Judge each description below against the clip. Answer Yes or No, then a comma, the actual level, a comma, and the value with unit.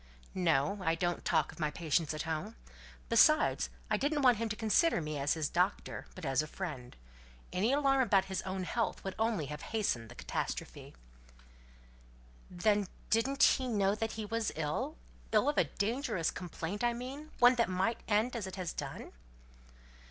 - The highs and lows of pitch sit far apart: Yes, wide, 5.8 semitones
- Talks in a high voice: Yes, high, 205 Hz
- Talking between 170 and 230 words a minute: Yes, average, 175 wpm